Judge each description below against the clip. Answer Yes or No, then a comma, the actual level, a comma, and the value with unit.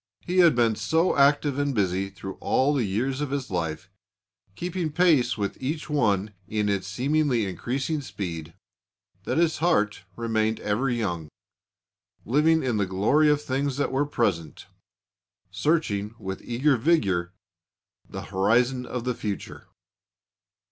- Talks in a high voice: No, low, 120 Hz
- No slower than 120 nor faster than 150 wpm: Yes, average, 140 wpm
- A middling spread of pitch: No, wide, 6.4 semitones